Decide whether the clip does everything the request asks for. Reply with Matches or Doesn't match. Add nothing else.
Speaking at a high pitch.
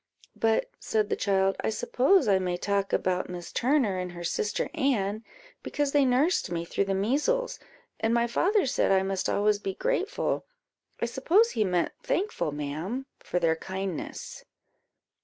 Matches